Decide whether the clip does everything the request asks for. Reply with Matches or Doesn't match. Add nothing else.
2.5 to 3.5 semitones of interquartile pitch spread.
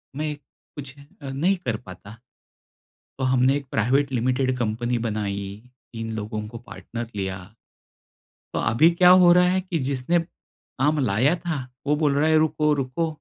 Doesn't match